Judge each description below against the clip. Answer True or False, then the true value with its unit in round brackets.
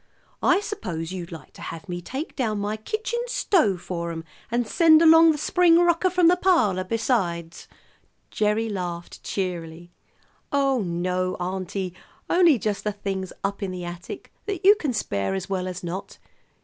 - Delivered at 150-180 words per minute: True (165 wpm)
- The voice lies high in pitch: True (200 Hz)